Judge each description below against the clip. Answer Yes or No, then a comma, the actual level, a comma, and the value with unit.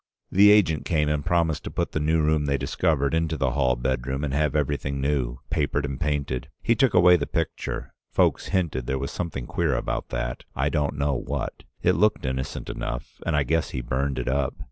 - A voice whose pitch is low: Yes, very low, 70 Hz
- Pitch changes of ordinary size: Yes, average, 3.2 semitones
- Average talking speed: No, fast, 210 wpm